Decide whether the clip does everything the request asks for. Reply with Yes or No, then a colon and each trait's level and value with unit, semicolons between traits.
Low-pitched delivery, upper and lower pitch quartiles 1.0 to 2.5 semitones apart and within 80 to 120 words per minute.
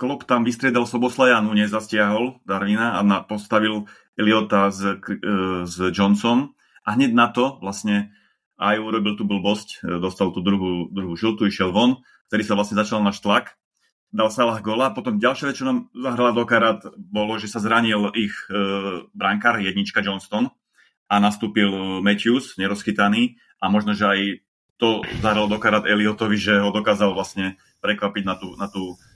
No: low, 105 Hz; narrow, 2.2 semitones; average, 150 wpm